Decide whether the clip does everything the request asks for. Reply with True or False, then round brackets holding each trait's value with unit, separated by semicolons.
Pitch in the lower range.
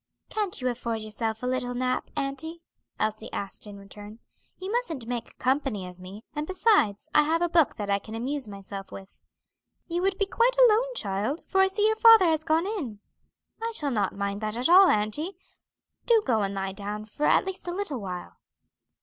False (255 Hz)